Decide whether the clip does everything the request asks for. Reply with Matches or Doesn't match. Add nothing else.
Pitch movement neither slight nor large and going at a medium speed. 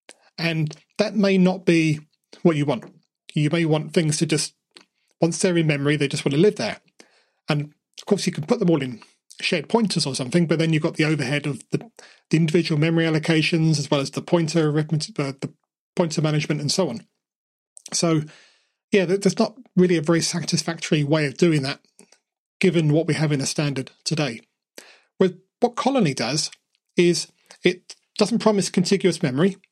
Matches